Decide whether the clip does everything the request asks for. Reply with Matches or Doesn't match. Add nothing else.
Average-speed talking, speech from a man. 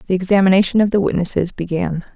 Doesn't match